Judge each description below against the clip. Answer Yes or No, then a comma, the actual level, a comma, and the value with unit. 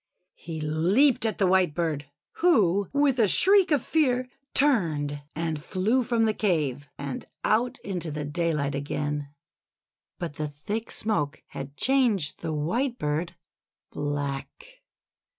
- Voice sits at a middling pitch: Yes, medium, 175 Hz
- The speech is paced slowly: Yes, slow, 130 wpm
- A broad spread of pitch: Yes, wide, 8.4 semitones